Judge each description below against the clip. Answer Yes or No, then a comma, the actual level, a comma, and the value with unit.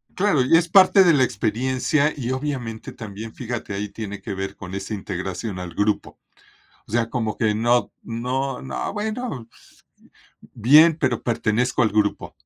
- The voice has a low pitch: Yes, low, 115 Hz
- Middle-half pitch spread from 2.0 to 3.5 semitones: No, average, 4.2 semitones